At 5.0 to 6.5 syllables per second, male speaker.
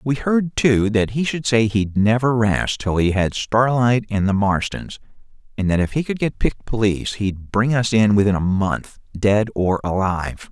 No: 4.6 syllables/s; male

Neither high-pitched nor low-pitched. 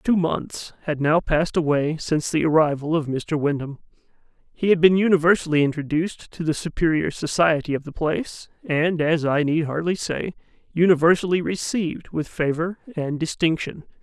Yes: medium, 160 Hz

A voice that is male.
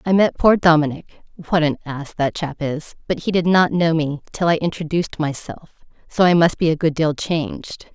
No: female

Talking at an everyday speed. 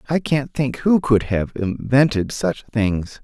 Yes: average, 165 wpm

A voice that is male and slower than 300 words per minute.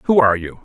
Yes: male; fast, 280 wpm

